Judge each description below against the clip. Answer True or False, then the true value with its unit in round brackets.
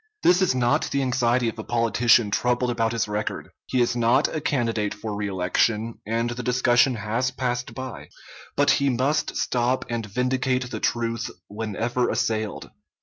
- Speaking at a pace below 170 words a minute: True (160 wpm)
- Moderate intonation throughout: False (2.1 semitones)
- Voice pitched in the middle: False (120 Hz)